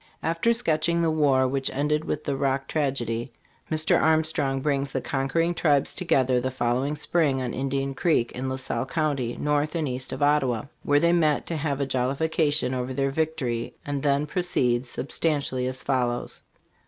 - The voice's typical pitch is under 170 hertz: Yes, medium, 140 Hz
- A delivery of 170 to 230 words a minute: Yes, average, 180 wpm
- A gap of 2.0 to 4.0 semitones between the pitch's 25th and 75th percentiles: Yes, average, 3.1 semitones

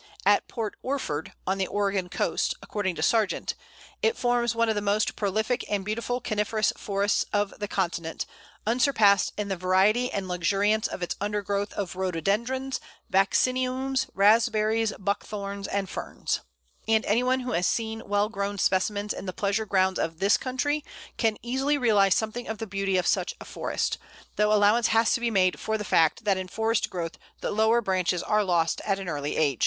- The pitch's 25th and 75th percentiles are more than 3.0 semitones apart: No, average, 2.7 semitones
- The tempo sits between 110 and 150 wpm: No, average, 180 wpm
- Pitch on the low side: No, high, 205 Hz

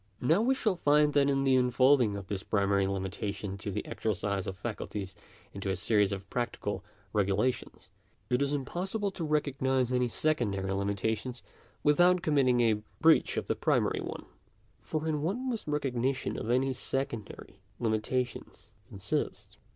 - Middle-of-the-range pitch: No, low, 125 Hz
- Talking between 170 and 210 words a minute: No, average, 150 wpm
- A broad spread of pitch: Yes, wide, 6.3 semitones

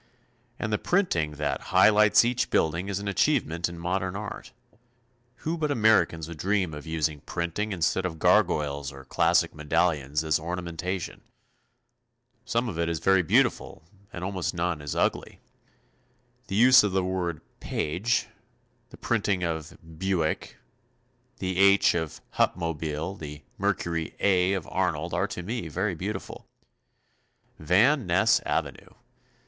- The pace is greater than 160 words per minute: No, average, 140 wpm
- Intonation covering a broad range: No, average, 3.8 semitones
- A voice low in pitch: Yes, very low, 90 Hz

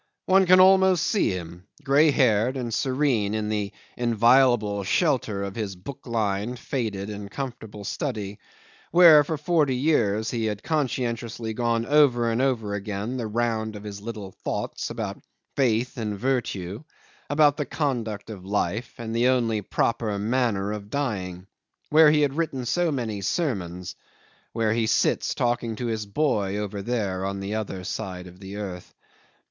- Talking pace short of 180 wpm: Yes, average, 160 wpm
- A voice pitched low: Yes, low, 115 Hz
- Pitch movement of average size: Yes, average, 4.3 semitones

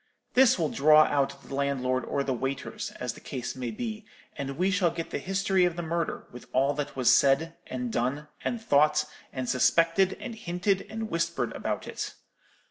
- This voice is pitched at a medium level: Yes, medium, 150 Hz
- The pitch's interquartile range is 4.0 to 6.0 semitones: Yes, average, 5.0 semitones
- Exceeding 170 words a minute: Yes, average, 190 wpm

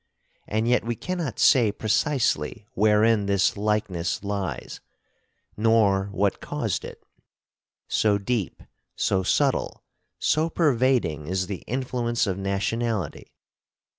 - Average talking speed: No, slow, 105 wpm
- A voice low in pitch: Yes, low, 105 Hz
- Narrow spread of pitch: No, average, 3.3 semitones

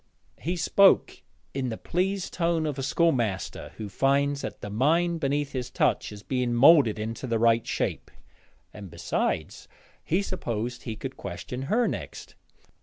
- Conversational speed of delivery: Yes, average, 155 wpm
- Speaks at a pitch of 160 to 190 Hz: No, low, 135 Hz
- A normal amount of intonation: No, wide, 6.2 semitones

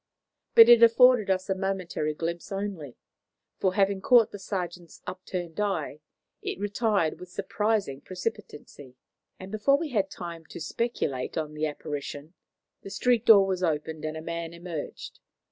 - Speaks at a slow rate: No, average, 150 wpm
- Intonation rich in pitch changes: No, average, 4.4 semitones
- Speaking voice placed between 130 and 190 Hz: Yes, medium, 185 Hz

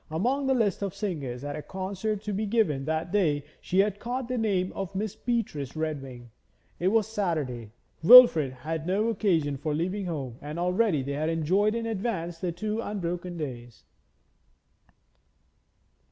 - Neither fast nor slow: Yes, average, 160 wpm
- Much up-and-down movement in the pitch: Yes, wide, 5.7 semitones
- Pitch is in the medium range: Yes, medium, 180 Hz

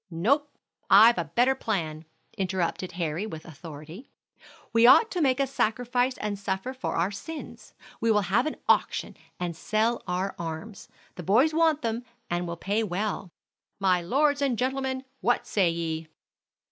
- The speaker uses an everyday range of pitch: No, wide, 6.4 semitones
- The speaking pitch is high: Yes, high, 210 Hz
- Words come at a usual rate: Yes, average, 160 wpm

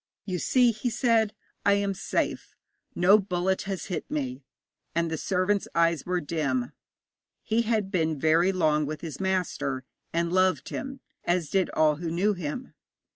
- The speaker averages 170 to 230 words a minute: No, average, 160 wpm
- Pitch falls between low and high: Yes, medium, 180 Hz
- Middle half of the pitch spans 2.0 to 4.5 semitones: Yes, average, 4.2 semitones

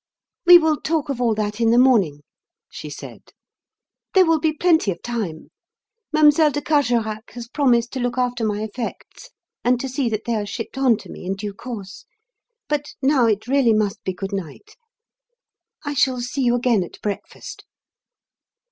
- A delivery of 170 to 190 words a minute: Yes, average, 175 wpm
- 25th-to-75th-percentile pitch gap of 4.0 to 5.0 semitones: Yes, average, 4.7 semitones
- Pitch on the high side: Yes, high, 240 Hz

